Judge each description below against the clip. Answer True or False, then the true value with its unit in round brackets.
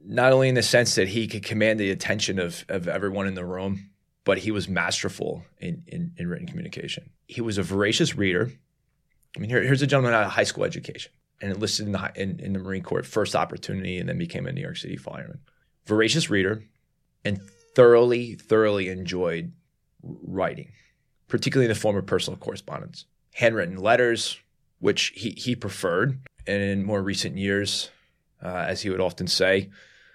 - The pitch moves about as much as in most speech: False (5.8 semitones)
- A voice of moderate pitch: False (110 Hz)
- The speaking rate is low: False (185 wpm)